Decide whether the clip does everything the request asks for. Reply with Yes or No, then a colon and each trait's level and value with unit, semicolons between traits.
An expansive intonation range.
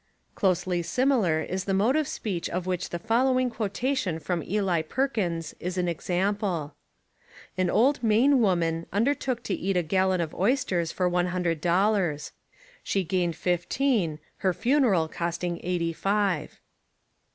No: average, 4.3 semitones